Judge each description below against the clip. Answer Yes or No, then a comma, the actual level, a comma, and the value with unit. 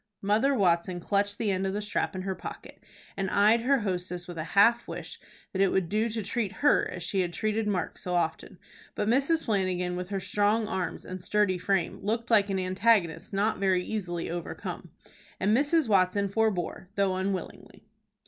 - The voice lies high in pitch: Yes, high, 195 Hz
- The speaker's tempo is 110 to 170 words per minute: No, average, 185 wpm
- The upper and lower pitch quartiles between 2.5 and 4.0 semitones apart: Yes, average, 2.8 semitones